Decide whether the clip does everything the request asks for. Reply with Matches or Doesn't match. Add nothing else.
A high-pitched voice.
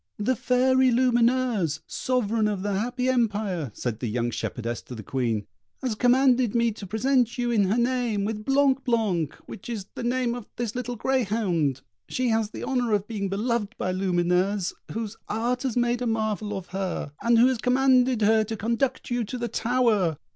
Matches